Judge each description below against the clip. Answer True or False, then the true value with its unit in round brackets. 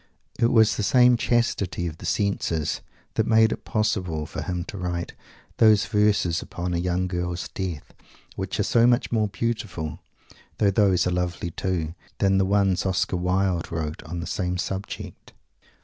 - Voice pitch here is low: True (90 Hz)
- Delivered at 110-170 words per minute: True (165 wpm)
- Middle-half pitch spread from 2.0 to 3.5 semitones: True (3.1 semitones)